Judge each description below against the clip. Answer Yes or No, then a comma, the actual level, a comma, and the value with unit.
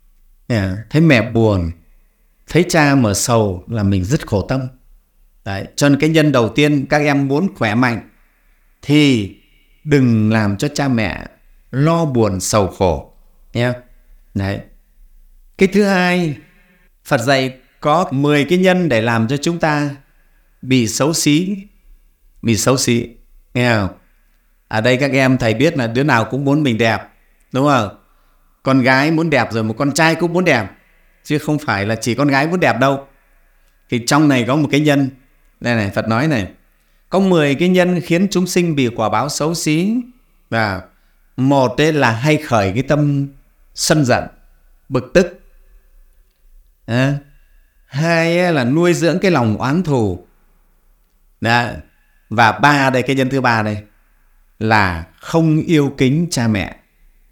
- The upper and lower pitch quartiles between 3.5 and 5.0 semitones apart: No, wide, 5.4 semitones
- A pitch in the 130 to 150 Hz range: Yes, low, 135 Hz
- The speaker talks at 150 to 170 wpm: Yes, slow, 165 wpm